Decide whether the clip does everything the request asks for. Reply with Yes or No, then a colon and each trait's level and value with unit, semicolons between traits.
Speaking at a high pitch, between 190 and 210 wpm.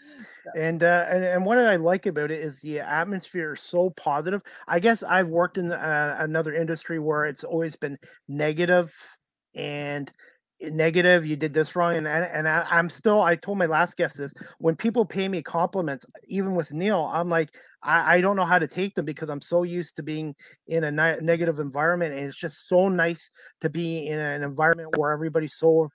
No: medium, 165 Hz; average, 200 wpm